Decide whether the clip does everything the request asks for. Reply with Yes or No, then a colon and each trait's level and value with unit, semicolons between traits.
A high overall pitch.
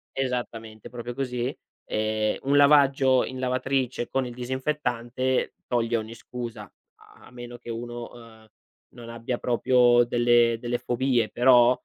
No: low, 120 Hz